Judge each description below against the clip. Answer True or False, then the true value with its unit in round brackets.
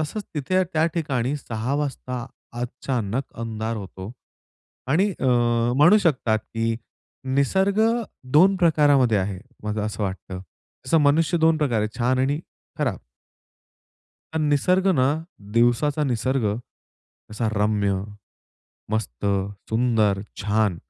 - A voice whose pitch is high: False (125 Hz)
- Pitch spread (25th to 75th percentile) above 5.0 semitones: True (5.4 semitones)